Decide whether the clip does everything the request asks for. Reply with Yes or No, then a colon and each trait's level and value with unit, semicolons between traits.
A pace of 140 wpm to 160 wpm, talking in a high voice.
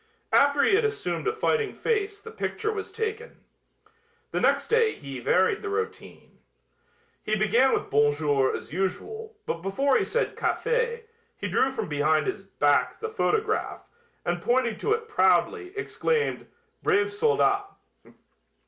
Yes: average, 150 wpm; very high, 410 Hz